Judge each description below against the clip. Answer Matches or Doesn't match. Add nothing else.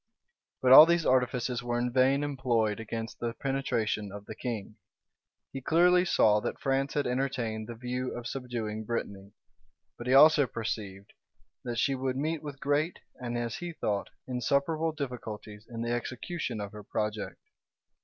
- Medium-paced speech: Matches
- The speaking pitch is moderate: Doesn't match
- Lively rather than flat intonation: Doesn't match